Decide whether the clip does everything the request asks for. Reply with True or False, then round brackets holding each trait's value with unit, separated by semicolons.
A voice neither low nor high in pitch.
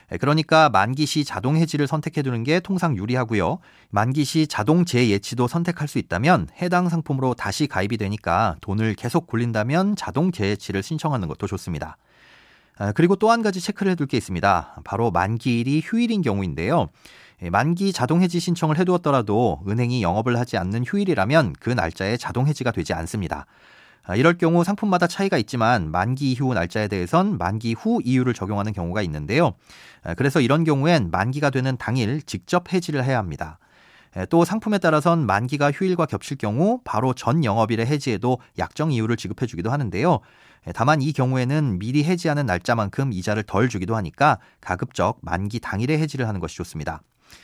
False (125 Hz)